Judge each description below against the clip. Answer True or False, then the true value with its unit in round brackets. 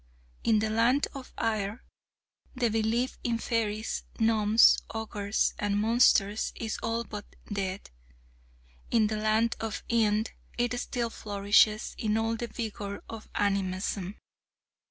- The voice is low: False (220 Hz)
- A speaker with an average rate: False (125 wpm)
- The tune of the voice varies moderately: False (1.8 semitones)